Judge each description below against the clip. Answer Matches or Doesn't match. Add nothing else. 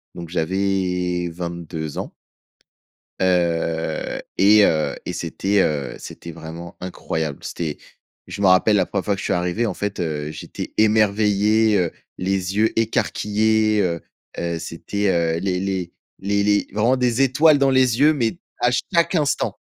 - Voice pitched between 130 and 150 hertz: Doesn't match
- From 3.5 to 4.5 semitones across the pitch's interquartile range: Matches